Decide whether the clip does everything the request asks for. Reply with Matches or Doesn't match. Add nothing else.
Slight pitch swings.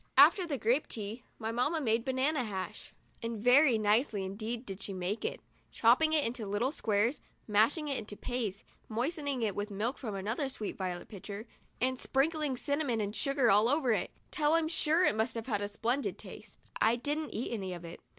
Doesn't match